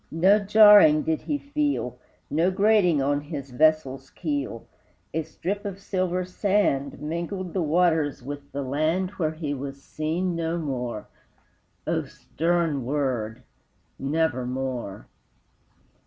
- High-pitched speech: No, medium, 155 Hz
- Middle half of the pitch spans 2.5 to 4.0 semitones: No, average, 4.8 semitones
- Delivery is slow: Yes, slow, 120 wpm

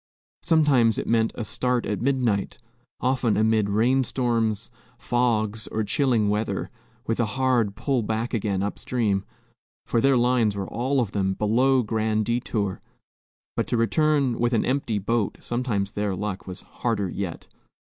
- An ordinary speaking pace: Yes, average, 150 wpm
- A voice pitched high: No, low, 115 Hz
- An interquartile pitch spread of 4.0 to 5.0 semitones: No, average, 3.1 semitones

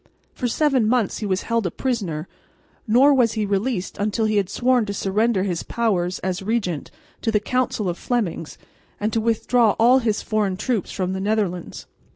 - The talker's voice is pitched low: No, high, 215 Hz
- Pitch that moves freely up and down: No, average, 3.7 semitones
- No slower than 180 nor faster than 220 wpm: Yes, average, 185 wpm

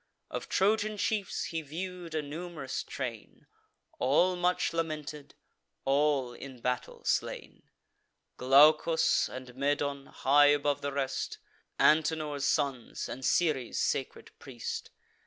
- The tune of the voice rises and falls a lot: No, average, 3.2 semitones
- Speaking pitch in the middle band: Yes, medium, 145 Hz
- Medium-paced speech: No, slow, 110 wpm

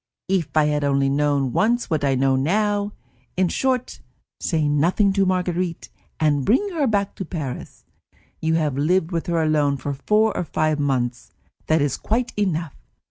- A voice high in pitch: No, medium, 160 Hz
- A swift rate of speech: No, average, 170 wpm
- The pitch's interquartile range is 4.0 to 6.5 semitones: Yes, wide, 5.5 semitones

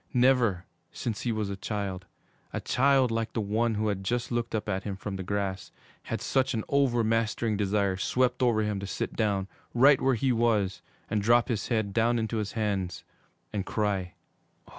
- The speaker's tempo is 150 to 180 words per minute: No, average, 190 wpm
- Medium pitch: No, low, 110 Hz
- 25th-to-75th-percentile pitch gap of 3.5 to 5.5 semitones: No, average, 3.0 semitones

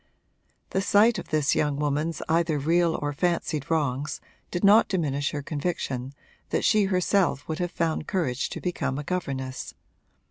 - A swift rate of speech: No, average, 155 wpm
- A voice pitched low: No, medium, 155 Hz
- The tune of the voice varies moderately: Yes, average, 3.8 semitones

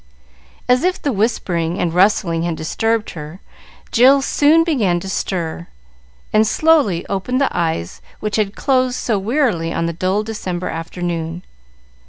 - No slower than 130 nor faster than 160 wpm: Yes, average, 145 wpm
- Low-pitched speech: No, high, 195 Hz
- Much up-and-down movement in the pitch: Yes, wide, 6.7 semitones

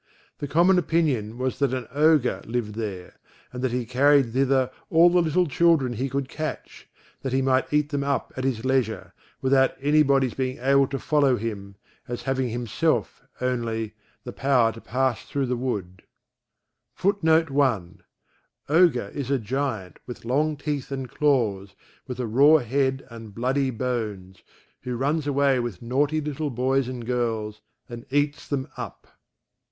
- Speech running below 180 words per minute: Yes, average, 160 wpm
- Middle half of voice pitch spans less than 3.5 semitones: Yes, average, 3.1 semitones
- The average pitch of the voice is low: Yes, low, 130 Hz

